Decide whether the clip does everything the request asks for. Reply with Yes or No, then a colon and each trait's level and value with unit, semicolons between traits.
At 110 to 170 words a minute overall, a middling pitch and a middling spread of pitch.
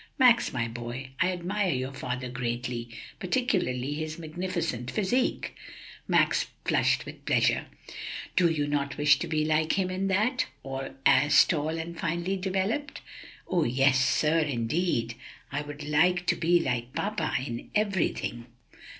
No: slow, 135 wpm; medium, 155 Hz; wide, 6.0 semitones